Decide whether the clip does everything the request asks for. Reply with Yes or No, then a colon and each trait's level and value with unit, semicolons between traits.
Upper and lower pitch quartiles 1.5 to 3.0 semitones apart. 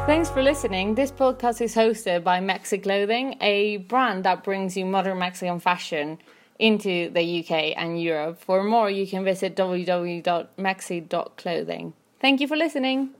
No: average, 4.7 semitones